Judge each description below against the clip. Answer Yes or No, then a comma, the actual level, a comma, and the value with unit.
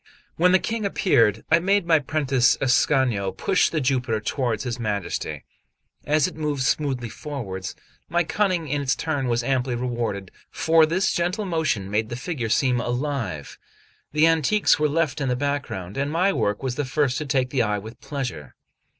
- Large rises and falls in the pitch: No, average, 5.0 semitones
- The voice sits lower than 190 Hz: Yes, low, 135 Hz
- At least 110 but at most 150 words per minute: No, average, 175 wpm